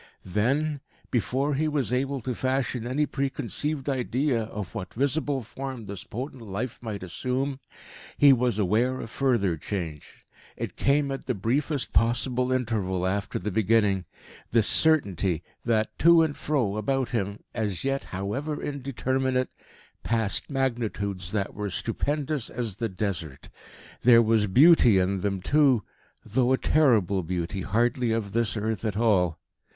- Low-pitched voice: Yes, low, 115 Hz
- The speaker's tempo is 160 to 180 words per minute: No, average, 145 wpm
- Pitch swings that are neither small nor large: Yes, average, 4.9 semitones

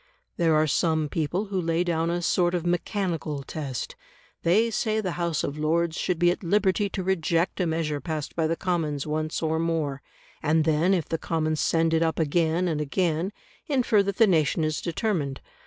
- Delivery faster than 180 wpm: Yes, average, 190 wpm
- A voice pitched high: No, medium, 165 Hz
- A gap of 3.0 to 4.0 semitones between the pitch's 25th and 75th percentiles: No, narrow, 2.4 semitones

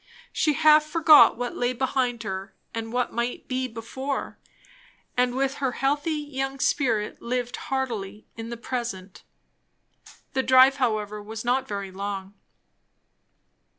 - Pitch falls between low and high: No, high, 245 Hz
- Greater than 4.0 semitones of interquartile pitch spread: No, average, 3.5 semitones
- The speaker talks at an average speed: No, slow, 130 wpm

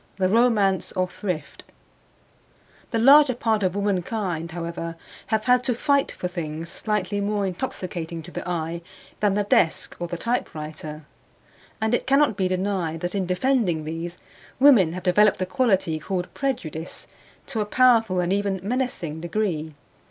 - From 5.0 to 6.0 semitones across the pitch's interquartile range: No, average, 4.5 semitones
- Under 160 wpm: Yes, average, 150 wpm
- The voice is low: No, high, 190 Hz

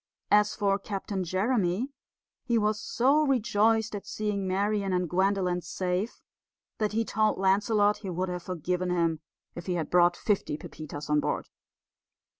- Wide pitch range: No, average, 3.0 semitones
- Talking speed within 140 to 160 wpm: Yes, average, 150 wpm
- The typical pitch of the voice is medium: No, high, 195 Hz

